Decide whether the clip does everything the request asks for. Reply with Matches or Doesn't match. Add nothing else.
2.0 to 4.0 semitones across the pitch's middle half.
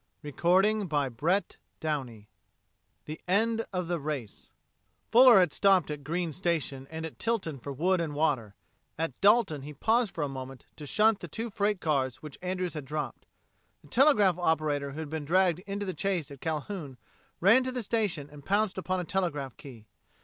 Doesn't match